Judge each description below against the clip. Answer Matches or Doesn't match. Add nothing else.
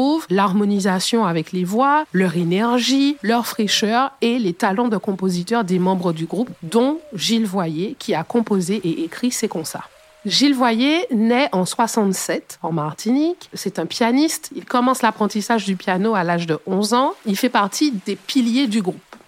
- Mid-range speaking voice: Doesn't match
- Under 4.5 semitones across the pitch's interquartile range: Doesn't match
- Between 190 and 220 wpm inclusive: Doesn't match